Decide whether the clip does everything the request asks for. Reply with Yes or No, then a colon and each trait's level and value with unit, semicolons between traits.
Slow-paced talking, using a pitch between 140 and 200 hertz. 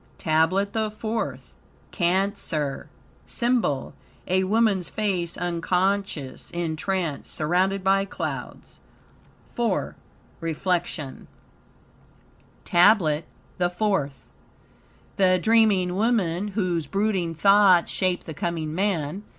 Yes: slow, 90 wpm; medium, 185 Hz